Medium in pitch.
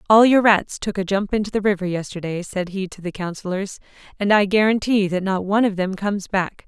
No: high, 195 Hz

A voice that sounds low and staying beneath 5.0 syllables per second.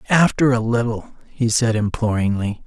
Yes: low, 115 Hz; 4.8 syllables/s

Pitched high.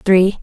Yes: high, 195 Hz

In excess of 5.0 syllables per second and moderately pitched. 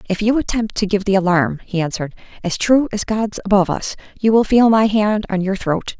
No: 5.6 syllables/s; high, 205 Hz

